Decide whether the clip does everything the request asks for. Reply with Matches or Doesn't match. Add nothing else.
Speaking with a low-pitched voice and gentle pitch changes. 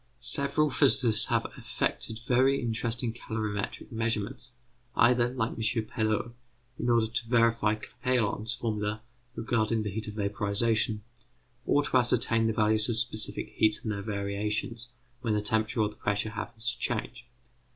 Matches